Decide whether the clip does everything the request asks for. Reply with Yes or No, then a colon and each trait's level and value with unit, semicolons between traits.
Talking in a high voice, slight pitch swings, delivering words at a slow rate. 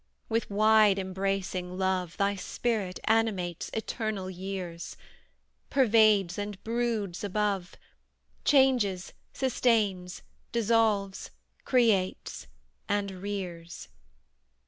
No: high, 200 Hz; average, 3.0 semitones; slow, 80 wpm